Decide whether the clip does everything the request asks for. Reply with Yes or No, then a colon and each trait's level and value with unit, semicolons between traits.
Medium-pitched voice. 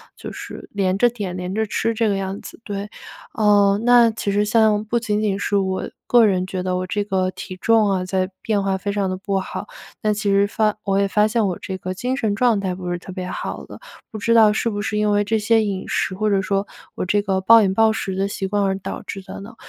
No: high, 200 Hz